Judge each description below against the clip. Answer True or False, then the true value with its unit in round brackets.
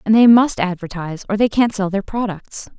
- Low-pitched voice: False (205 Hz)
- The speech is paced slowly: False (215 wpm)